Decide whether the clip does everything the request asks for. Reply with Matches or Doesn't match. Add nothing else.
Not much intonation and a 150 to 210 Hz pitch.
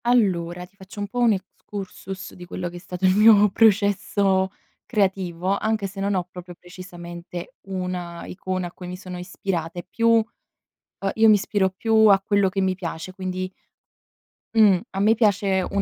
Matches